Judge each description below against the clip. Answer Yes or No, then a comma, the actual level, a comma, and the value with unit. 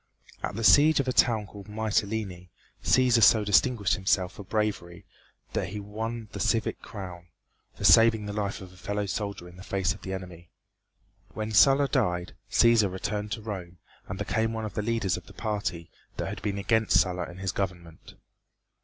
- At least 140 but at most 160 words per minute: No, average, 185 wpm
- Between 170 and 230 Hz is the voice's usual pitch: No, low, 105 Hz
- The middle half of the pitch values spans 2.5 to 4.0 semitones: Yes, average, 3.1 semitones